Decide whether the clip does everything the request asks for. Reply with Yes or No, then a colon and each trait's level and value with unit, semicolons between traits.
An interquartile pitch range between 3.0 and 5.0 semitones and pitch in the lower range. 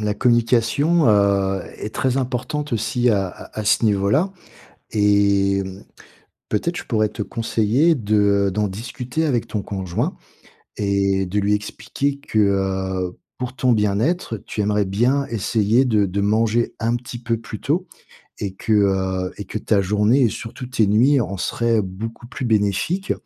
Yes: average, 3.5 semitones; low, 105 Hz